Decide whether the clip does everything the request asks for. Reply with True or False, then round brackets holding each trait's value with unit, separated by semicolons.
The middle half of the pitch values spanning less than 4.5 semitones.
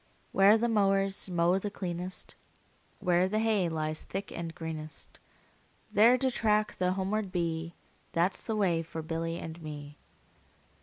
True (3.6 semitones)